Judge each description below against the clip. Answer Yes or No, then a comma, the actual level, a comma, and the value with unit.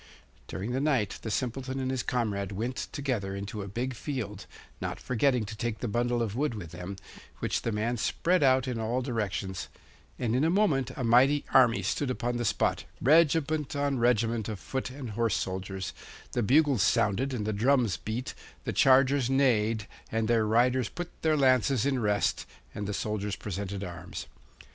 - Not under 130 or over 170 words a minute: No, average, 180 wpm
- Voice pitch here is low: Yes, low, 120 Hz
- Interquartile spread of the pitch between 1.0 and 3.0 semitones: No, average, 4.1 semitones